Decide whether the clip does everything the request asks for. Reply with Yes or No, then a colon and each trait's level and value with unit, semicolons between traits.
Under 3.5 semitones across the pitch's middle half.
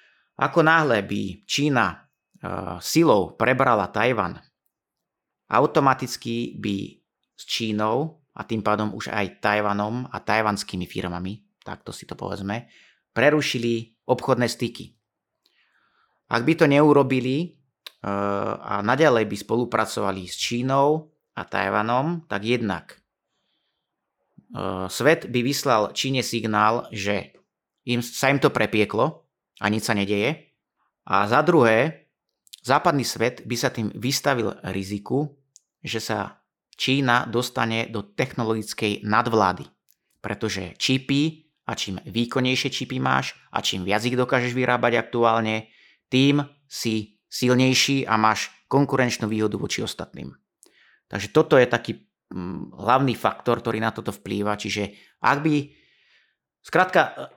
No: average, 4.0 semitones